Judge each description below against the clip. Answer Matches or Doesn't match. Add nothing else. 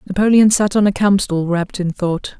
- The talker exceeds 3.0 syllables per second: Matches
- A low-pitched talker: Doesn't match